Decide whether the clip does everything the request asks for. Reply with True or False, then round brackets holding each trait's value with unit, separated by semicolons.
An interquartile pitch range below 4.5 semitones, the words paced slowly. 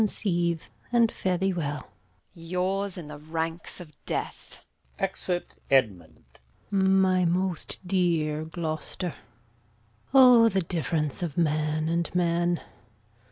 True (3.2 semitones; 115 wpm)